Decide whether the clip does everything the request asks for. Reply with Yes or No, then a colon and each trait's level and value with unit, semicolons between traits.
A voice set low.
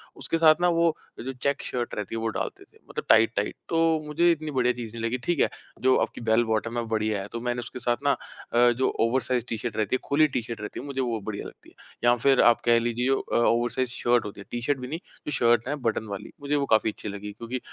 Yes: low, 120 Hz